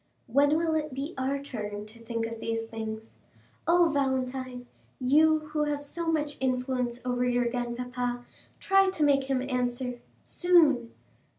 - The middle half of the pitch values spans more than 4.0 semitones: No, average, 3.4 semitones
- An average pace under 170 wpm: Yes, average, 140 wpm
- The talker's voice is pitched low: No, very high, 255 Hz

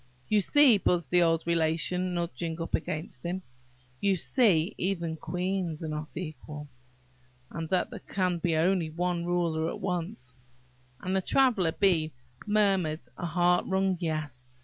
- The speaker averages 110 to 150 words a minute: Yes, average, 145 wpm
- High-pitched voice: No, medium, 170 Hz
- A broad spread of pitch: No, average, 2.8 semitones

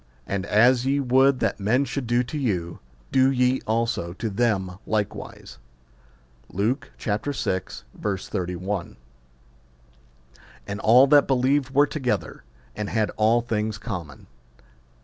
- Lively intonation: No, average, 4.6 semitones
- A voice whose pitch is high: No, low, 115 Hz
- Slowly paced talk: Yes, slow, 120 wpm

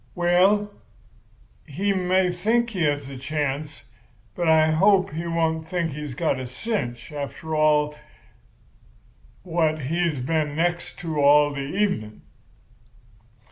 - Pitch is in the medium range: Yes, medium, 160 Hz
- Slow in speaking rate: Yes, slow, 120 wpm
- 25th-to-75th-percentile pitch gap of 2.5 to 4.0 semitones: Yes, average, 3.6 semitones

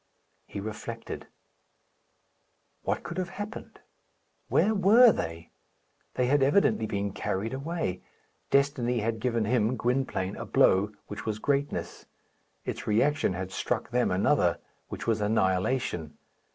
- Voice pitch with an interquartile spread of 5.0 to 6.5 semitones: Yes, wide, 5.4 semitones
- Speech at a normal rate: No, slow, 125 wpm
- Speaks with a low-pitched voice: Yes, low, 115 Hz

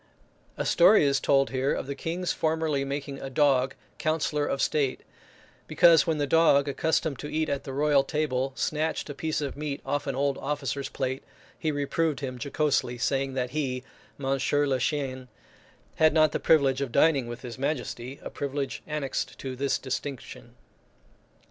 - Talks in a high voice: No, medium, 140 Hz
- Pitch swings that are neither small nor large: No, narrow, 2.2 semitones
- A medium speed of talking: Yes, average, 170 wpm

